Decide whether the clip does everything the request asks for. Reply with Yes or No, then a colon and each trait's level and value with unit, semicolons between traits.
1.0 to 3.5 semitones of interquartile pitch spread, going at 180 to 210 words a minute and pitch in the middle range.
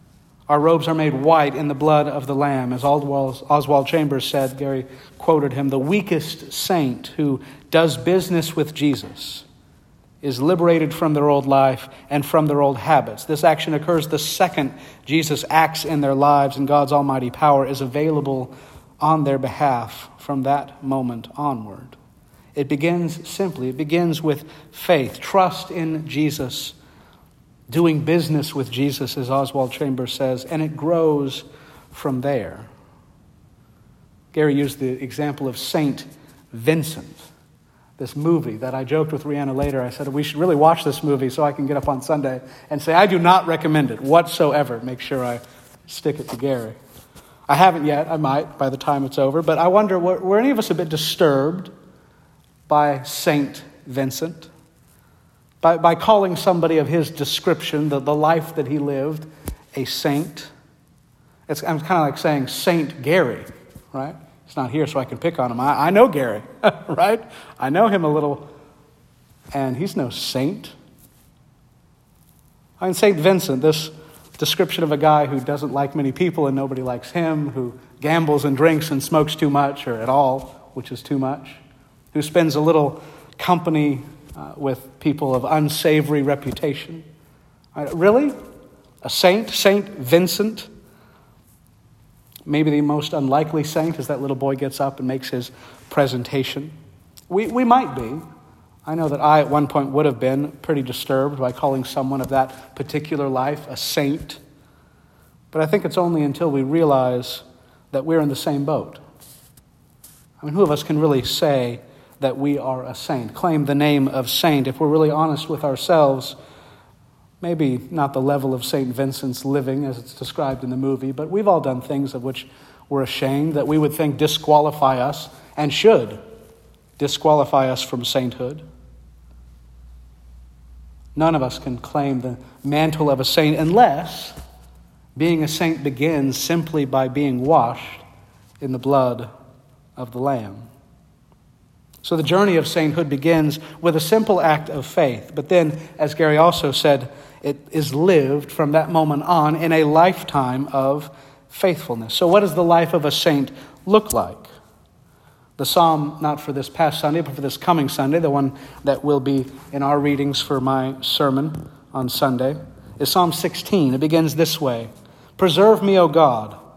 No: average, 2.8 semitones; average, 165 wpm; medium, 145 Hz